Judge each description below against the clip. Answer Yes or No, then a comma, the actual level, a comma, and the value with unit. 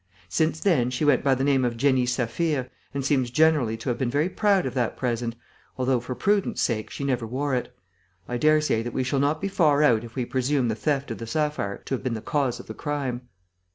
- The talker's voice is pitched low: Yes, low, 130 Hz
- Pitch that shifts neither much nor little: Yes, average, 3.4 semitones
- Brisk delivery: Yes, fast, 235 wpm